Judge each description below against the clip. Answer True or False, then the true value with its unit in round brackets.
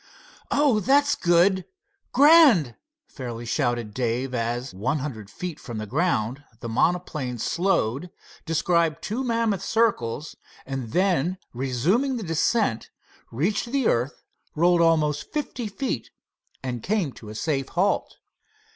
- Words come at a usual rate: False (120 wpm)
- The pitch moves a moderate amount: False (9.0 semitones)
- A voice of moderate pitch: True (165 Hz)